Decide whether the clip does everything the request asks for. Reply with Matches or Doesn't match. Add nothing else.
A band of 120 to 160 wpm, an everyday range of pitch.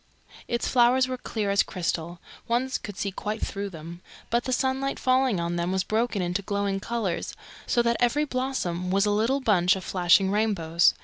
Doesn't match